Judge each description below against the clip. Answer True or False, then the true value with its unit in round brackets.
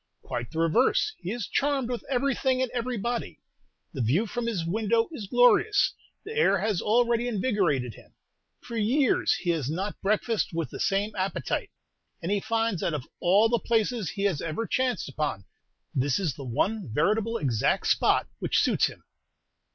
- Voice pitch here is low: False (210 Hz)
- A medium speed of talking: True (170 wpm)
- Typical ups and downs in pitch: False (6.3 semitones)